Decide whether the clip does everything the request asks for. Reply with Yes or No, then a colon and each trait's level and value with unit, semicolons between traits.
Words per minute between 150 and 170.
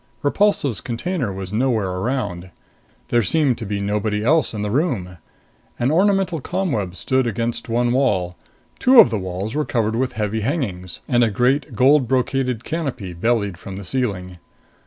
Yes: average, 160 wpm